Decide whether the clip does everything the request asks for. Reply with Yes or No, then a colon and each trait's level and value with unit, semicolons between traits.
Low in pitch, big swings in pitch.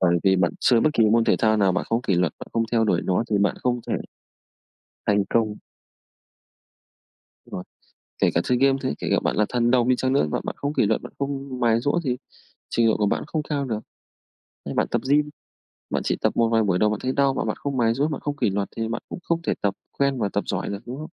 No: low, 115 Hz; average, 4.6 semitones